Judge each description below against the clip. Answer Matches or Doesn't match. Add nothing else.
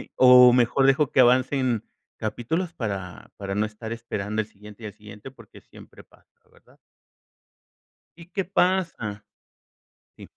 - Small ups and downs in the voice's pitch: Doesn't match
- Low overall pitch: Matches